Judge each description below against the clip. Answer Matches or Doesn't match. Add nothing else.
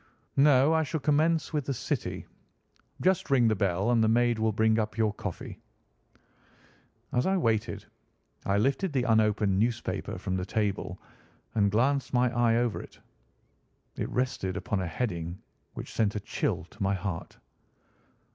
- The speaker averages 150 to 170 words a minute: Matches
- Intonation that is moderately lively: Matches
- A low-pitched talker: Matches